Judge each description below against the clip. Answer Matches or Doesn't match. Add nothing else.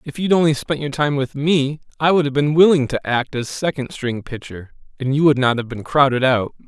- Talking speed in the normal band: Doesn't match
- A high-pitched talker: Doesn't match